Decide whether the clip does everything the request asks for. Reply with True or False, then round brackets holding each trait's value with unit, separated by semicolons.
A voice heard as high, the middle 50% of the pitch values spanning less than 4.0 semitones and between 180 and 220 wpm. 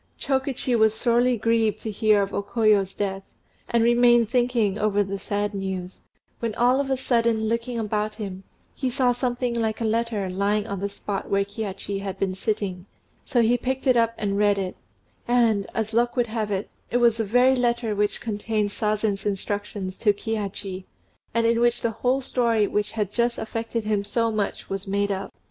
True (220 Hz; 2.7 semitones; 190 wpm)